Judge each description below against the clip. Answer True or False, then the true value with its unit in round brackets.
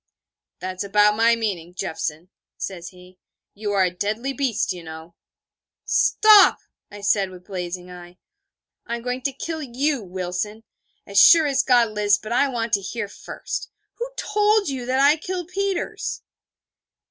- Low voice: False (215 Hz)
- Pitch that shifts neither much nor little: False (6.7 semitones)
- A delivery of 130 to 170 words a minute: True (160 wpm)